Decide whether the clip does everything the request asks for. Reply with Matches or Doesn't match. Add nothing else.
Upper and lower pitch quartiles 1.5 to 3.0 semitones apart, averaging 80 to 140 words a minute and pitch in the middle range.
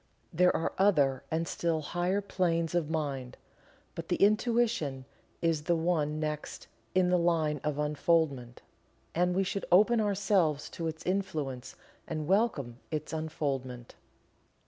Doesn't match